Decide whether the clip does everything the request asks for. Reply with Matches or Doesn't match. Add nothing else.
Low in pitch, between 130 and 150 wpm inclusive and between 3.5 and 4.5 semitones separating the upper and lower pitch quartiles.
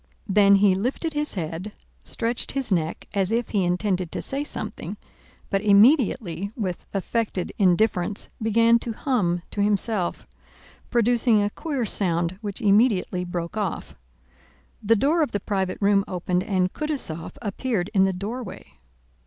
Doesn't match